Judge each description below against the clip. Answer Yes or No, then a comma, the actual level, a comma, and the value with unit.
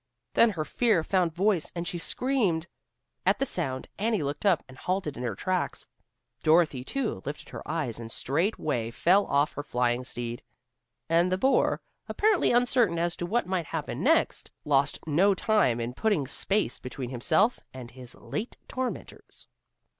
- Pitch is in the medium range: Yes, medium, 165 Hz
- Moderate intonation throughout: No, wide, 7.6 semitones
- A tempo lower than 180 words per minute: Yes, average, 160 wpm